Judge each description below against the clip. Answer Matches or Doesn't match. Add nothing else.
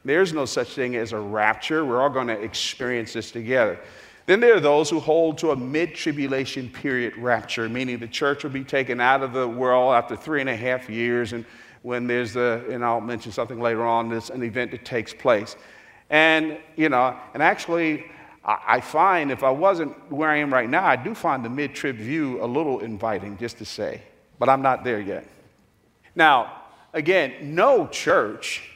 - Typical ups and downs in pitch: Matches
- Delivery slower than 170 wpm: Doesn't match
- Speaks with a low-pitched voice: Matches